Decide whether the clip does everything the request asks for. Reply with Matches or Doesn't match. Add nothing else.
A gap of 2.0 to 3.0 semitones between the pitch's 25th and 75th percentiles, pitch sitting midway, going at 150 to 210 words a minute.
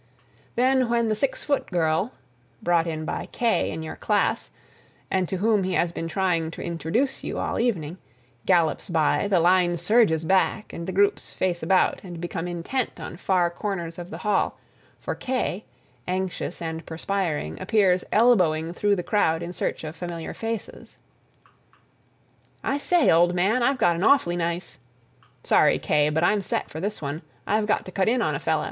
Doesn't match